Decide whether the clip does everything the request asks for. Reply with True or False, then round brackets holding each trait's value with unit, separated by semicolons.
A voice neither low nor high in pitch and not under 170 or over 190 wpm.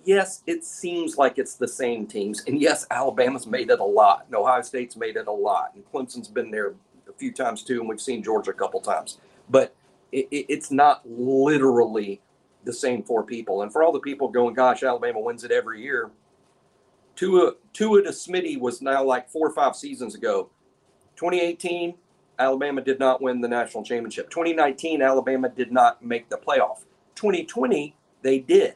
True (150 Hz; 185 wpm)